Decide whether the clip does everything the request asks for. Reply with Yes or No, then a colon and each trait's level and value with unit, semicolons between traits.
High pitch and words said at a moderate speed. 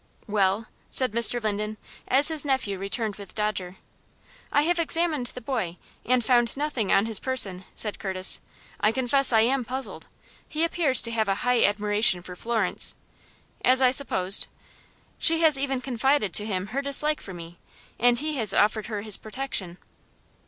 Yes: high, 230 Hz; average, 170 wpm